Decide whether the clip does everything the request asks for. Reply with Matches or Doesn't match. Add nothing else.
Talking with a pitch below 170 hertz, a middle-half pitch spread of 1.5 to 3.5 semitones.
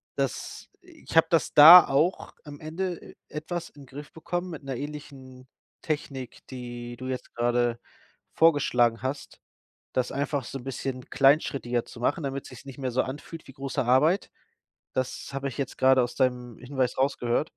Matches